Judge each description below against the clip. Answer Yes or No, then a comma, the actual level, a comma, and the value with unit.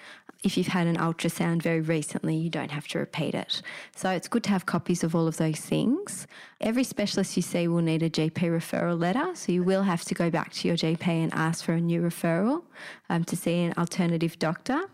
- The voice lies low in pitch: No, medium, 170 Hz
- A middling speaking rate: No, fast, 225 wpm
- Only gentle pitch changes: Yes, narrow, 2.0 semitones